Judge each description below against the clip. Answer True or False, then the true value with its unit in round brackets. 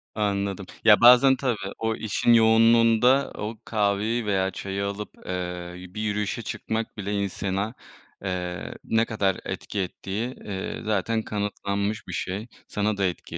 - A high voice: False (105 Hz)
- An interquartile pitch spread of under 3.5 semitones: True (2.4 semitones)